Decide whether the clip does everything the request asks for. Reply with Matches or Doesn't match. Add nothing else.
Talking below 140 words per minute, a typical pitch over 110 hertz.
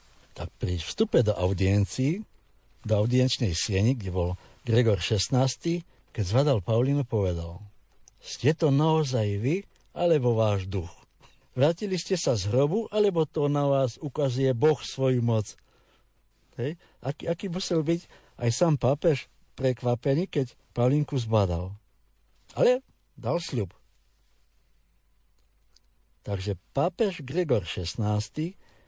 Matches